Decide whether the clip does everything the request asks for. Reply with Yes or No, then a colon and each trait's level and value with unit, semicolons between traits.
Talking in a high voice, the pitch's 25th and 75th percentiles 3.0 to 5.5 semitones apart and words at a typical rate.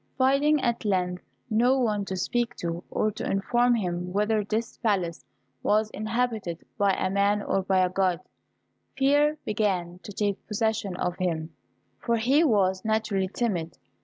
Yes: high, 205 Hz; average, 4.0 semitones; average, 155 wpm